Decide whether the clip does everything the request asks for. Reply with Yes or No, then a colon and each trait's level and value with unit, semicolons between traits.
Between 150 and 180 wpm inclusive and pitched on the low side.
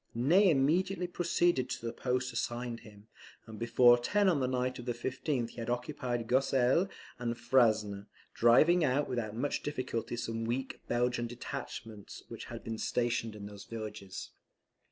Yes: average, 155 wpm; low, 120 Hz